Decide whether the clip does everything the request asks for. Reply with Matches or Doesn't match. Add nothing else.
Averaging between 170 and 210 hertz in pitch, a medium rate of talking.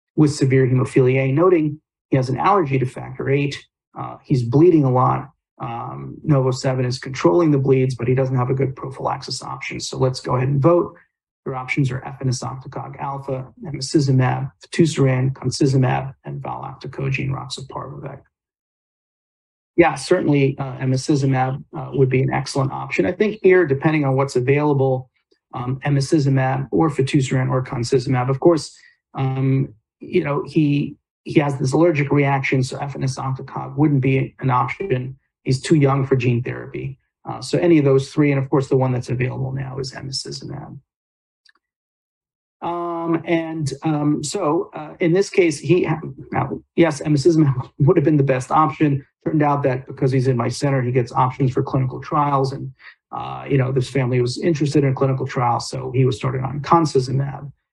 Doesn't match